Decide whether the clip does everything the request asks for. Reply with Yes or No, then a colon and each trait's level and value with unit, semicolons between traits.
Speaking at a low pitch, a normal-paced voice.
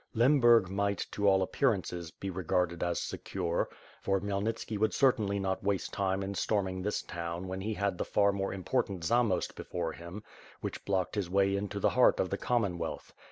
Yes: low, 100 Hz; average, 180 wpm